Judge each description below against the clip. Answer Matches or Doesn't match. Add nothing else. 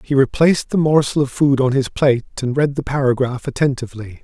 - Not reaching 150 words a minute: Doesn't match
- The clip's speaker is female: Doesn't match